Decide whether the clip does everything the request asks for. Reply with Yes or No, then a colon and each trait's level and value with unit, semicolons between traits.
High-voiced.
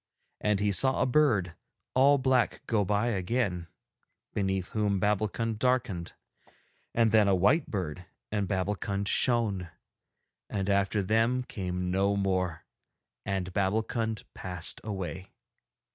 No: low, 100 Hz